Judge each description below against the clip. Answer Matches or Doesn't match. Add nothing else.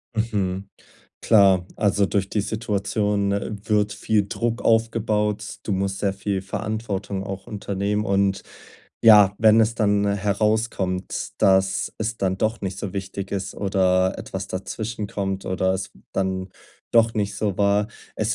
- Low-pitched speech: Matches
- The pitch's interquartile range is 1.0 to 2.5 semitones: Matches